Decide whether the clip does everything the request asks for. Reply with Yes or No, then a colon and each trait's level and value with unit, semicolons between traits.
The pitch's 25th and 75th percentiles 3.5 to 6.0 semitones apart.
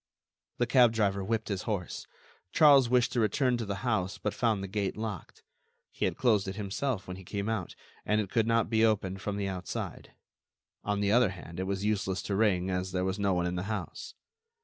No: average, 2.8 semitones